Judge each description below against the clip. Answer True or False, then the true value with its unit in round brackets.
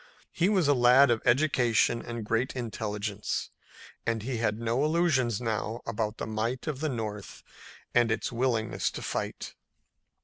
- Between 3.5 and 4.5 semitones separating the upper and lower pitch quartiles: False (2.9 semitones)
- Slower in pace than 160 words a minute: True (150 wpm)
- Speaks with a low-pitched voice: True (120 Hz)